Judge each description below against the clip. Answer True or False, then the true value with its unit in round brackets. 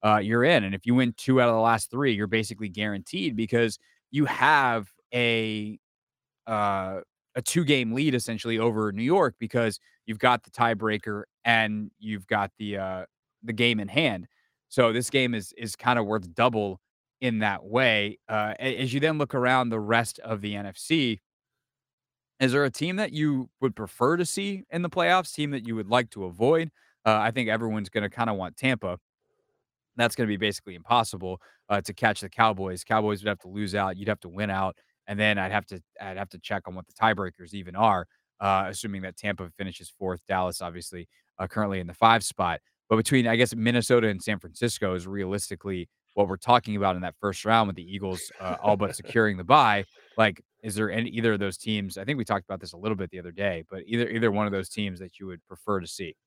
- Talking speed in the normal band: False (220 wpm)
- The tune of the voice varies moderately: True (3.3 semitones)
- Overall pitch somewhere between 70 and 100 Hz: False (110 Hz)